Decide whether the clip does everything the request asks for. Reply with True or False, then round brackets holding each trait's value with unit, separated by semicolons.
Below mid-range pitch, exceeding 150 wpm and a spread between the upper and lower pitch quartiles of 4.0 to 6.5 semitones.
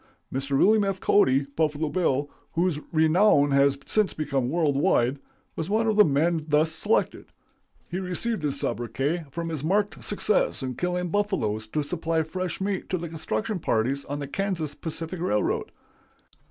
False (160 Hz; 160 wpm; 4.7 semitones)